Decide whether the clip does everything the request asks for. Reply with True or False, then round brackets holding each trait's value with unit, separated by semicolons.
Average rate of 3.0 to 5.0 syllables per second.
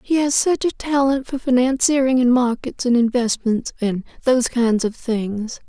True (4.6 syllables/s)